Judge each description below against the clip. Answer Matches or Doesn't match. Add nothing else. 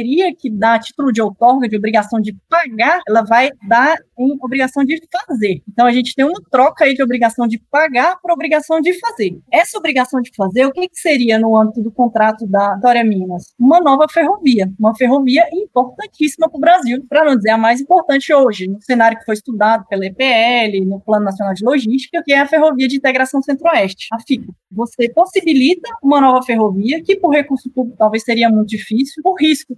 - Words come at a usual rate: Doesn't match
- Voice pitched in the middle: Doesn't match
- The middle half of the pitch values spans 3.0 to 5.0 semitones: Doesn't match